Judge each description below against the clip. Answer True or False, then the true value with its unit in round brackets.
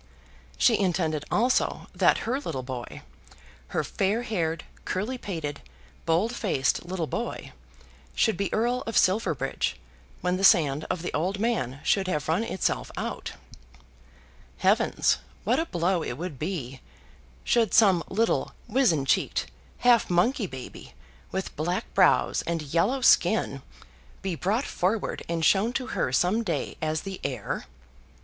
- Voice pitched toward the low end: False (185 Hz)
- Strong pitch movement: True (6.0 semitones)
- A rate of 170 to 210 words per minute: False (140 wpm)